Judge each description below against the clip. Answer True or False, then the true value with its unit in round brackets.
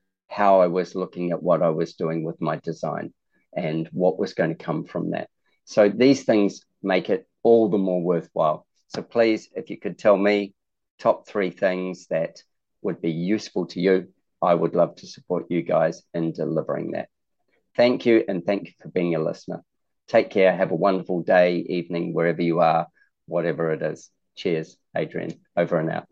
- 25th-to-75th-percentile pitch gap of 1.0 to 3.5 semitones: True (2.8 semitones)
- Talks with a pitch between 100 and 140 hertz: False (90 Hz)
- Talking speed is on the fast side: False (190 wpm)